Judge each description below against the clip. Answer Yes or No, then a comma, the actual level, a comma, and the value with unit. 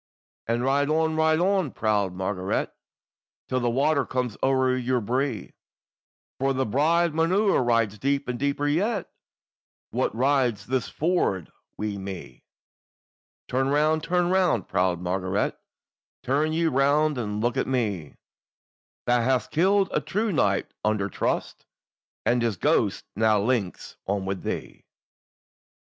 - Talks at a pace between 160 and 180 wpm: No, slow, 135 wpm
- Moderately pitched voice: No, low, 130 Hz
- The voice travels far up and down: Yes, wide, 6.5 semitones